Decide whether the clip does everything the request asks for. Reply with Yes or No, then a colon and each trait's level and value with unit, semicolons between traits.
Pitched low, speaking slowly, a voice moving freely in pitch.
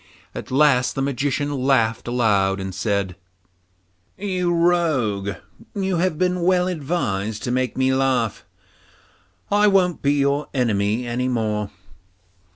Yes: low, 130 Hz; slow, 125 wpm; wide, 7.4 semitones